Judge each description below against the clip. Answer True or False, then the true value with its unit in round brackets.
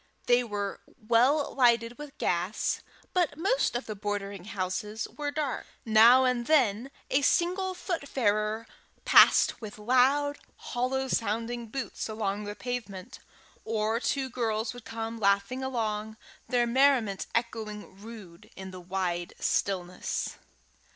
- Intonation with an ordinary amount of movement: True (3.9 semitones)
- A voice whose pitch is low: False (230 Hz)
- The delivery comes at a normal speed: False (130 wpm)